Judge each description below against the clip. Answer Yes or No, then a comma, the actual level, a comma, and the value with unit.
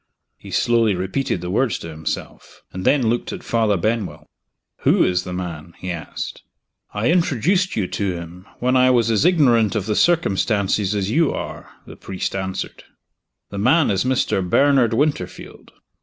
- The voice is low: Yes, low, 110 Hz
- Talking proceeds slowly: No, average, 165 wpm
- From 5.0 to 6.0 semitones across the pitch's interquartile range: Yes, wide, 5.6 semitones